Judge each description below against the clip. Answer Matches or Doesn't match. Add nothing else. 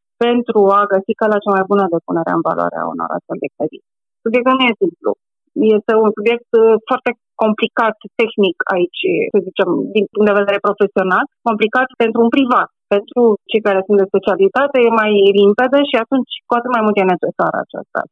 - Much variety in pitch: Doesn't match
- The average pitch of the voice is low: Doesn't match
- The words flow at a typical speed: Doesn't match